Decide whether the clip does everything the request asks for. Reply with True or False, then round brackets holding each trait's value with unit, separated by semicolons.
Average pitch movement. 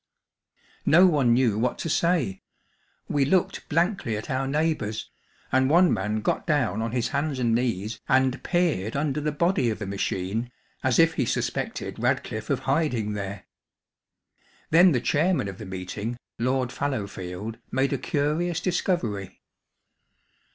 False (6.0 semitones)